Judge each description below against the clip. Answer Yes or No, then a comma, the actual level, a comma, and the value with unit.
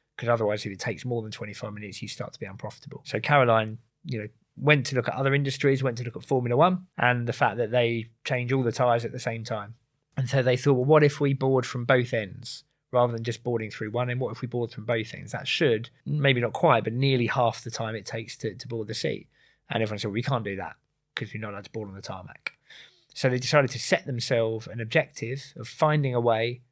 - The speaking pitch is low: Yes, low, 120 Hz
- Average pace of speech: No, fast, 260 wpm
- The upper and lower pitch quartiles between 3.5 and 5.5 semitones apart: No, average, 2.9 semitones